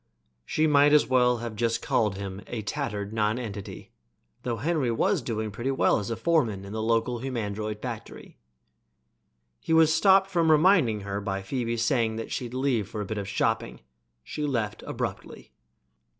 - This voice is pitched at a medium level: No, low, 115 Hz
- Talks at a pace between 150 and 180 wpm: Yes, average, 165 wpm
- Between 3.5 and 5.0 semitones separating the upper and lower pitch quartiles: Yes, average, 4.2 semitones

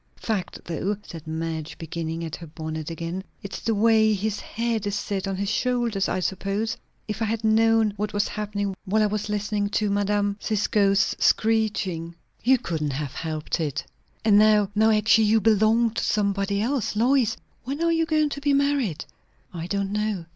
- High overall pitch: Yes, high, 205 Hz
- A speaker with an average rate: Yes, average, 180 wpm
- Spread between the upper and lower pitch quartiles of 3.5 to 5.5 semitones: No, average, 3.0 semitones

